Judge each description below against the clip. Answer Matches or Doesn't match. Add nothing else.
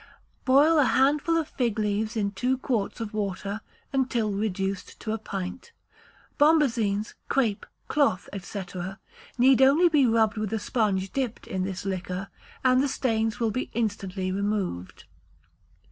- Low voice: Doesn't match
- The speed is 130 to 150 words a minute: Matches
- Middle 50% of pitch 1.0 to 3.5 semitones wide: Doesn't match